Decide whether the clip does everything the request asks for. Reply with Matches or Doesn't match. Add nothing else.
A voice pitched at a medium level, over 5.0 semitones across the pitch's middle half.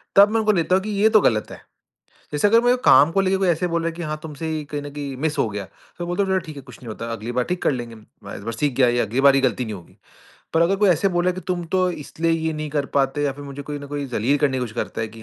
Matches